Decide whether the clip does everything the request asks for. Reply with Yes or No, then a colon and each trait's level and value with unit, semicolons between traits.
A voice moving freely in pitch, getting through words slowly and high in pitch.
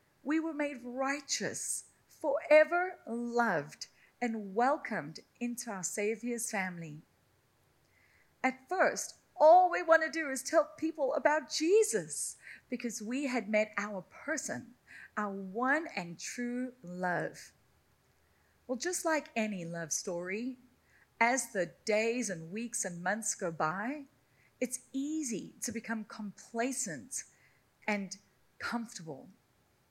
Yes: wide, 6.0 semitones; slow, 115 wpm; high, 240 Hz